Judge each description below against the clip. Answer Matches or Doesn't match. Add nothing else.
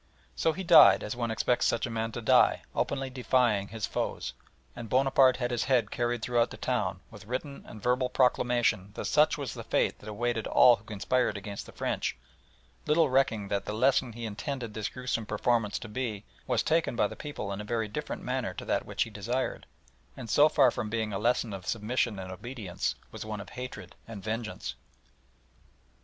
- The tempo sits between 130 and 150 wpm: Doesn't match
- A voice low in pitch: Matches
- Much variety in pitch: Doesn't match